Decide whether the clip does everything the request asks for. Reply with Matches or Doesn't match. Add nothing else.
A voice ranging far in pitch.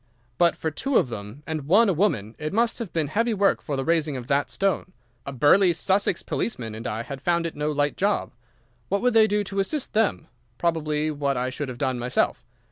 Matches